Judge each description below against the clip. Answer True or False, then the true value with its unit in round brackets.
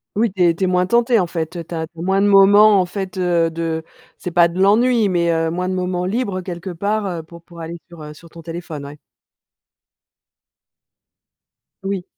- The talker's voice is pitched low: False (180 Hz)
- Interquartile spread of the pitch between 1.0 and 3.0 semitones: True (2.7 semitones)